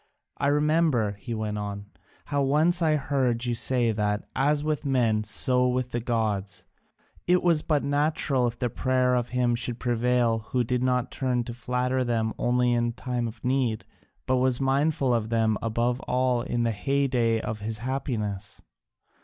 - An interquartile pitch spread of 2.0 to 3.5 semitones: Yes, narrow, 2.6 semitones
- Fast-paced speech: No, average, 170 wpm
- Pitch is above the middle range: No, low, 125 Hz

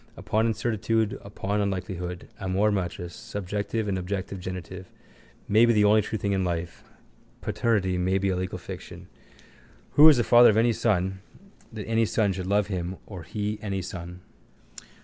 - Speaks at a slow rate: No, average, 165 wpm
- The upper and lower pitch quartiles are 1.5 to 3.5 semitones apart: Yes, average, 2.8 semitones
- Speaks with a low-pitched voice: Yes, low, 100 Hz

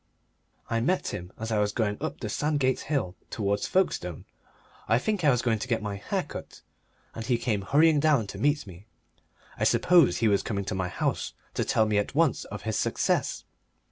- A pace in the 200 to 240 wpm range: Yes, fast, 205 wpm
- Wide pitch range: Yes, wide, 5.8 semitones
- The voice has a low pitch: Yes, low, 115 Hz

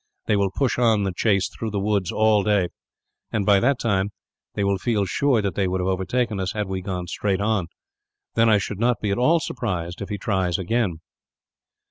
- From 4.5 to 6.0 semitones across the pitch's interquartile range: No, average, 2.8 semitones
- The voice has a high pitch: No, low, 100 Hz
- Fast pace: Yes, fast, 215 wpm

